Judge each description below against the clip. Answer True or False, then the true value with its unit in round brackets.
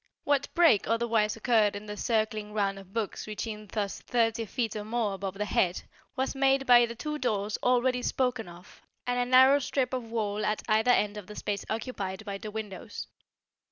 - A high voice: True (220 Hz)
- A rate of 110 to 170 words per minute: False (190 wpm)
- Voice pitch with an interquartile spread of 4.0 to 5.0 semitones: False (3.1 semitones)